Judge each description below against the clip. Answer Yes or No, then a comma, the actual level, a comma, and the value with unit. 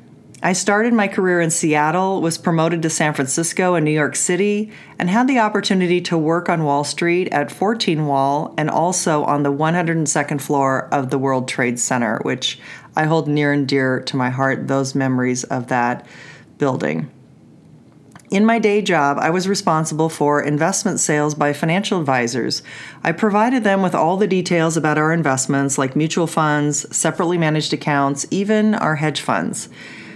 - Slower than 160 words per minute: No, average, 170 wpm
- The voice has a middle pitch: Yes, medium, 155 Hz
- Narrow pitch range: No, average, 4.2 semitones